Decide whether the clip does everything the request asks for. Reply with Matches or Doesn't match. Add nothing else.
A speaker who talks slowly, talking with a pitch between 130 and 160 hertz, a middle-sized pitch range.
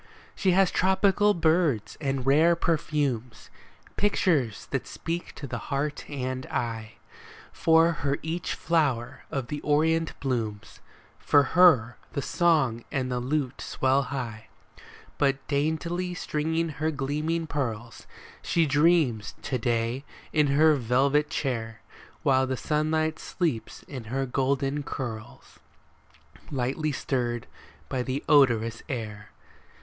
Matches